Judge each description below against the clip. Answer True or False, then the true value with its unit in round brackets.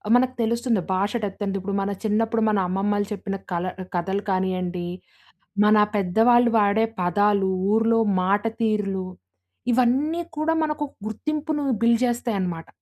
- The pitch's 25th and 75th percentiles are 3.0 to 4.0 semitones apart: True (3.5 semitones)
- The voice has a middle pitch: False (210 Hz)